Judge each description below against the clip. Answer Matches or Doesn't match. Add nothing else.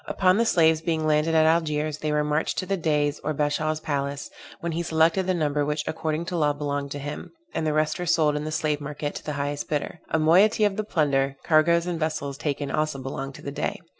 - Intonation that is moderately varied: Doesn't match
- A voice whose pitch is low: Doesn't match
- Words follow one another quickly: Matches